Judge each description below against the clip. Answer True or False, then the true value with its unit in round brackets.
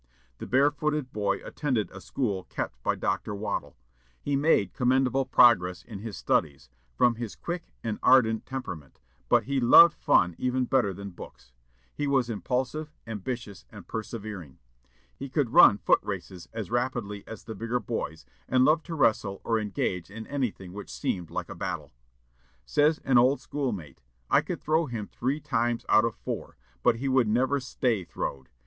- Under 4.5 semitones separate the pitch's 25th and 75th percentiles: False (4.9 semitones)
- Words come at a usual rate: True (165 wpm)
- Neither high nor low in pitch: False (115 Hz)